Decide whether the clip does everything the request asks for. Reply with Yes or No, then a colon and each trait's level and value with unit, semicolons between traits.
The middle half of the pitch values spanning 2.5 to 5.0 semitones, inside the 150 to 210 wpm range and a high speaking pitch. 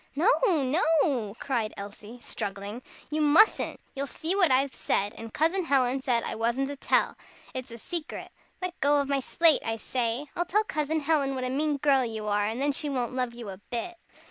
Yes: average, 4.5 semitones; average, 200 wpm; very high, 270 Hz